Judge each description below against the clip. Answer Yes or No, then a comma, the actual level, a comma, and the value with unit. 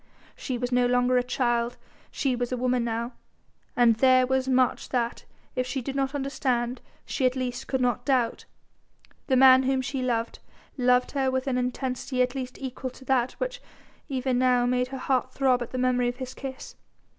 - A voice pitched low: No, very high, 255 Hz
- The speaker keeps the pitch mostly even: Yes, narrow, 1.1 semitones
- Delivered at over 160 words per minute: Yes, average, 190 wpm